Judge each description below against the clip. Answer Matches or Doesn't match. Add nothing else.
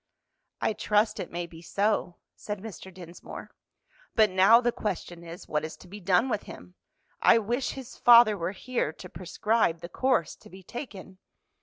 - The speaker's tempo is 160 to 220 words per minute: Matches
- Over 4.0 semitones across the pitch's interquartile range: Matches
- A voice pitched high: Matches